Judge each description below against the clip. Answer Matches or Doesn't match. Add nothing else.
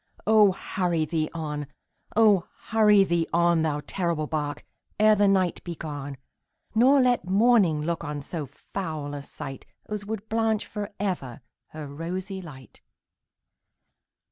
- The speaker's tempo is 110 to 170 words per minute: Matches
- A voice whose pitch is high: Doesn't match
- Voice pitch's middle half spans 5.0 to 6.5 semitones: Matches